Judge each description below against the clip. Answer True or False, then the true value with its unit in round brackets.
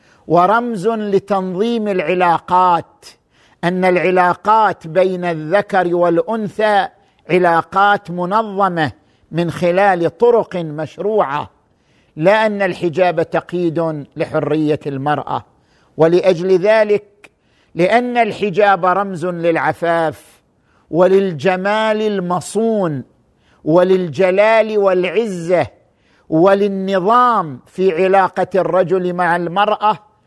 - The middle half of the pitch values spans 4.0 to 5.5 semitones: False (3.1 semitones)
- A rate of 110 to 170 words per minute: False (70 wpm)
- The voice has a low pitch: False (185 Hz)